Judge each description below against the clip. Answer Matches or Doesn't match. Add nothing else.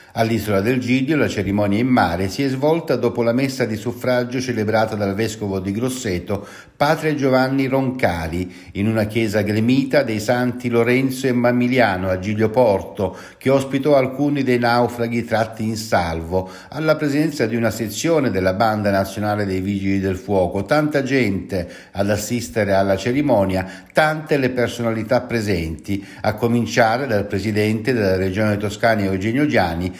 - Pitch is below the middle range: Matches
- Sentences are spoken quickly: Doesn't match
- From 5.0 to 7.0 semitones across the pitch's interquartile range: Doesn't match